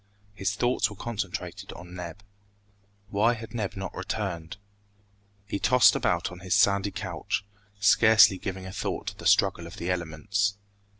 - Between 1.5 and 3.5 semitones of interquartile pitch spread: Yes, average, 2.7 semitones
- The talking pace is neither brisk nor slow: Yes, average, 155 wpm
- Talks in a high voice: No, low, 100 Hz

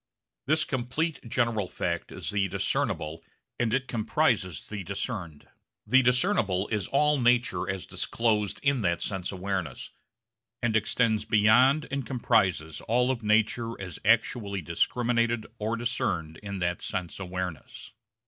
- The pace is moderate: No, slow, 130 wpm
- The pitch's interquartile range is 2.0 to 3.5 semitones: No, average, 4.7 semitones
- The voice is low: Yes, low, 110 Hz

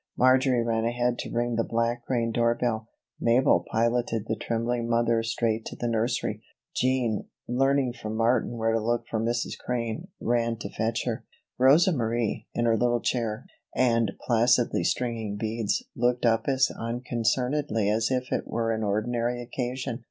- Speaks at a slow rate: No, average, 160 wpm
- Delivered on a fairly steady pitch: Yes, narrow, 1.4 semitones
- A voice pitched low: Yes, low, 115 Hz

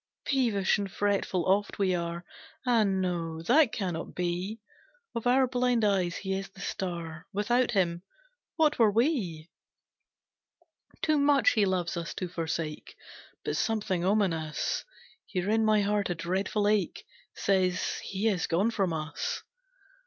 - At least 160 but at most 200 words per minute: No, average, 140 wpm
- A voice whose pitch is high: Yes, high, 195 Hz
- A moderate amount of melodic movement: Yes, average, 4.0 semitones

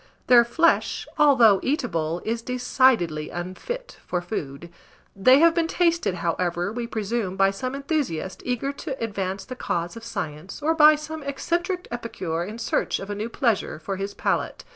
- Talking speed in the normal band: Yes, average, 165 wpm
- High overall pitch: Yes, high, 230 Hz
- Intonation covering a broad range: Yes, wide, 7.3 semitones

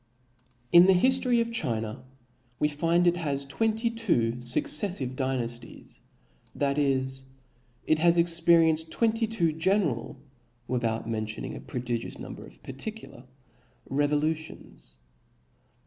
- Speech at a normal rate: No, slow, 120 wpm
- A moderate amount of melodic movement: No, wide, 5.9 semitones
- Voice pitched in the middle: Yes, medium, 150 Hz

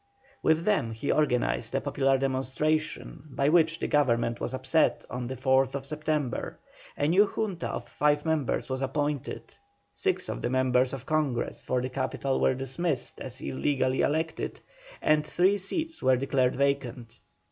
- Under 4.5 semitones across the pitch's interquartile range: Yes, average, 3.1 semitones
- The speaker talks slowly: No, average, 155 wpm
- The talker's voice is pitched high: No, low, 135 Hz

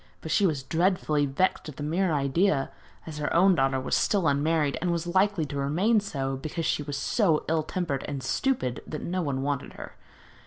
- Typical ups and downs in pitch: Yes, average, 4.5 semitones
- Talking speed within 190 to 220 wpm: Yes, average, 200 wpm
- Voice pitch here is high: No, medium, 155 Hz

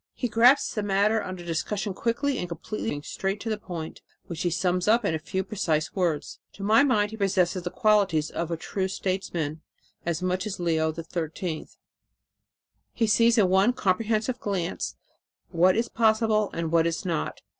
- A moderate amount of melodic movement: Yes, average, 4.0 semitones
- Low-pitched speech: No, high, 190 Hz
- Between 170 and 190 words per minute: Yes, average, 175 wpm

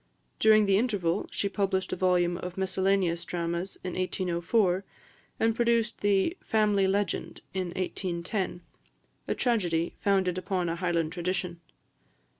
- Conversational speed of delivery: No, slow, 125 wpm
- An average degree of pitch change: No, narrow, 2.3 semitones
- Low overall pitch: No, medium, 185 Hz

